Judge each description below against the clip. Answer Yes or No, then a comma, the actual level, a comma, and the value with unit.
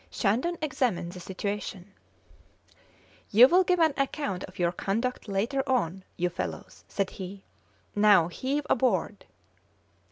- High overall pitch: Yes, high, 205 Hz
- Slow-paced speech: Yes, slow, 125 wpm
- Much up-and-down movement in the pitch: Yes, wide, 5.9 semitones